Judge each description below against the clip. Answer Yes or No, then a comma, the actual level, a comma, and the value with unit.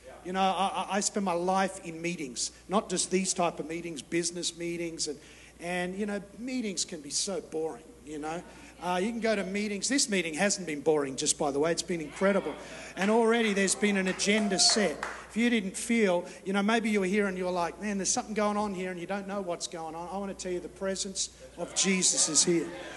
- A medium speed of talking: No, fast, 240 wpm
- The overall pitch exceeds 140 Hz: Yes, medium, 185 Hz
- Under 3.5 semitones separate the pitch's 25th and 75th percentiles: Yes, average, 3.0 semitones